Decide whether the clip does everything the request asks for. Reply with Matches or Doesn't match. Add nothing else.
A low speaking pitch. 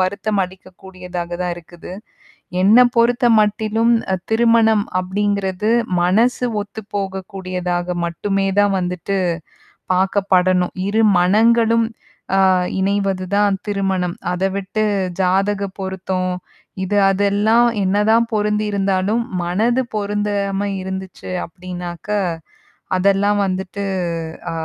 Doesn't match